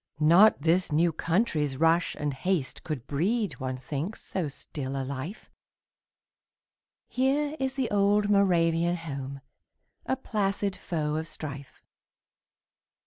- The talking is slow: Yes, slow, 120 wpm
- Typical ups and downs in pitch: No, wide, 5.8 semitones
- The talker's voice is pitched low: No, medium, 165 Hz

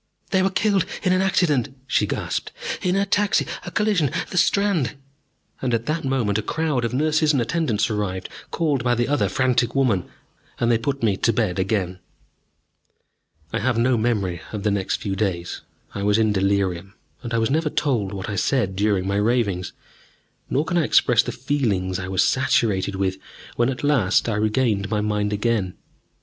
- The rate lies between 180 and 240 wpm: Yes, average, 190 wpm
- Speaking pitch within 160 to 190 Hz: No, low, 115 Hz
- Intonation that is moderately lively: No, wide, 5.8 semitones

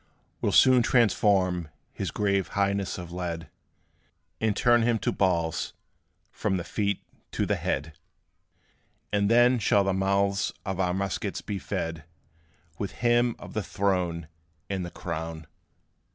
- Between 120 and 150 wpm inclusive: Yes, average, 140 wpm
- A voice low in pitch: Yes, very low, 95 Hz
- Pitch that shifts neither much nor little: Yes, average, 3.0 semitones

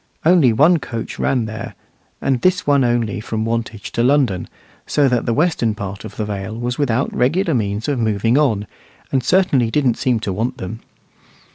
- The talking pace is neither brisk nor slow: Yes, average, 180 wpm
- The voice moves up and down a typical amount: Yes, average, 4.1 semitones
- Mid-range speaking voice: No, low, 120 Hz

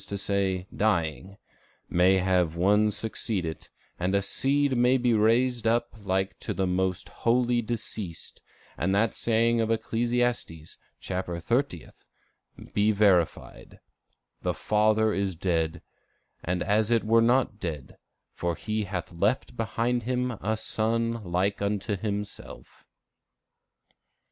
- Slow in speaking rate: Yes, slow, 125 wpm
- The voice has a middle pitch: No, low, 105 Hz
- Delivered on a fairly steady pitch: No, average, 3.8 semitones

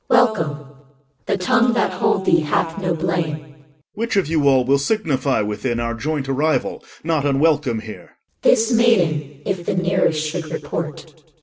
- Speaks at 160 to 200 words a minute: Yes, average, 170 wpm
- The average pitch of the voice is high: No, medium, 155 Hz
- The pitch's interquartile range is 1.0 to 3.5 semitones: No, average, 4.5 semitones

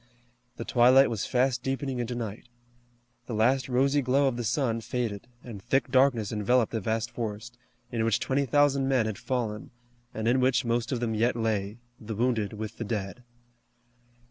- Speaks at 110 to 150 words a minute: No, average, 175 wpm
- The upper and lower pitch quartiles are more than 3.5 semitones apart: No, average, 2.7 semitones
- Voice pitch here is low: Yes, low, 120 Hz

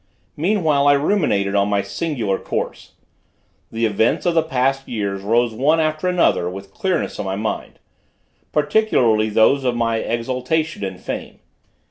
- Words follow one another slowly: No, average, 145 wpm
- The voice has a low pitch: Yes, low, 120 Hz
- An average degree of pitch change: No, wide, 7.0 semitones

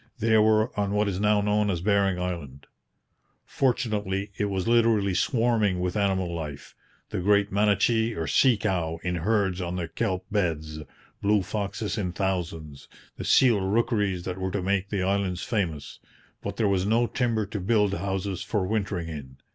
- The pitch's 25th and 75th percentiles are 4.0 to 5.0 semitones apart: No, average, 2.8 semitones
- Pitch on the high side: No, low, 100 Hz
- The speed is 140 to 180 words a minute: Yes, average, 170 wpm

